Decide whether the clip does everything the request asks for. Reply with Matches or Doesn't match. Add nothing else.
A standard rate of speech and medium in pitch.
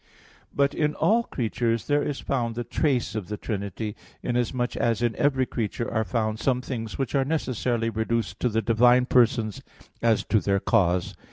Doesn't match